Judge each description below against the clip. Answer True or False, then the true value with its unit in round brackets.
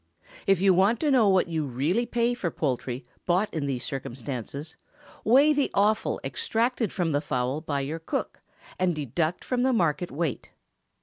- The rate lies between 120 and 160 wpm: False (170 wpm)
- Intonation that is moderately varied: False (7.6 semitones)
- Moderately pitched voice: True (170 Hz)